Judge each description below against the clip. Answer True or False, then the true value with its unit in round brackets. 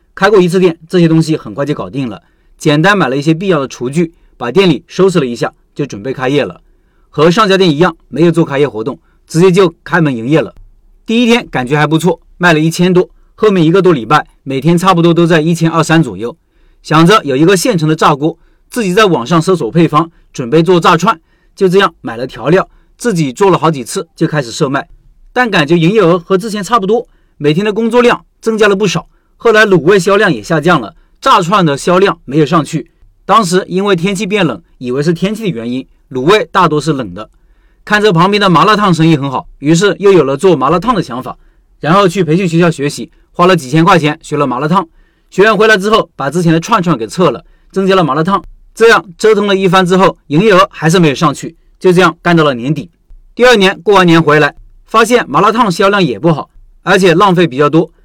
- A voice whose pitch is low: False (170 Hz)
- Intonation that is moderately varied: True (3.9 semitones)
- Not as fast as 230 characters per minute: False (330 characters per minute)